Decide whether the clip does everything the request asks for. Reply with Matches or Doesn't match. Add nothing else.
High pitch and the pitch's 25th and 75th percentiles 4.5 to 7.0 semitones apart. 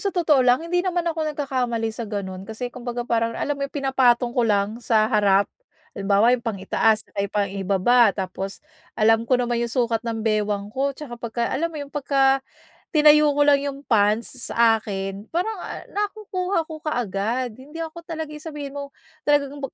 Matches